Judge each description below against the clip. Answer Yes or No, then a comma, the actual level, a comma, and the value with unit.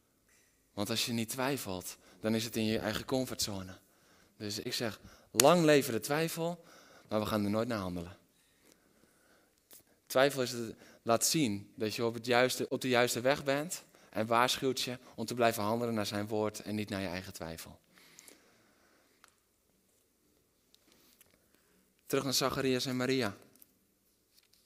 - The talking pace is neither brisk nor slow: Yes, average, 150 wpm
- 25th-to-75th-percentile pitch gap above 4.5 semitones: No, average, 3.9 semitones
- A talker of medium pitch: No, low, 115 Hz